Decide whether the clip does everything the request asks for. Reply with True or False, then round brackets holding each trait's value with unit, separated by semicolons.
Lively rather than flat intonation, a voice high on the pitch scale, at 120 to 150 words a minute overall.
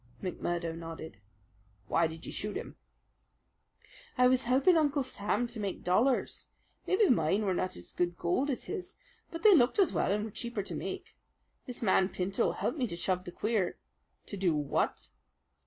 False (6.4 semitones; 205 Hz; 180 wpm)